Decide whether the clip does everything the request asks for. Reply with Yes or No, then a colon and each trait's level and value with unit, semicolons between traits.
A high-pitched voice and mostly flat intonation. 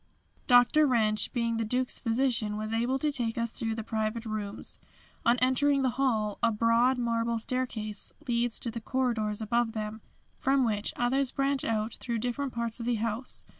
Yes: high, 235 Hz; narrow, 2.3 semitones